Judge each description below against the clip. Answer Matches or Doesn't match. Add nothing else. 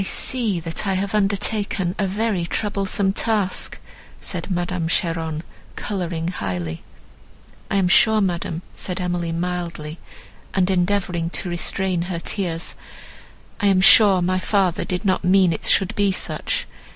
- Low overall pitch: Doesn't match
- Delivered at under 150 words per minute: Matches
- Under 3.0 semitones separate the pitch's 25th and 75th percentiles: Matches